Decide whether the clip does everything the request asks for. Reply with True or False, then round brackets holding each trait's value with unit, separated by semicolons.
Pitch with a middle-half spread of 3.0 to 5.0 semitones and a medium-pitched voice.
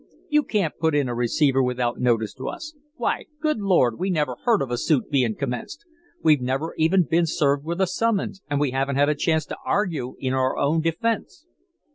False (5.5 semitones; 150 Hz)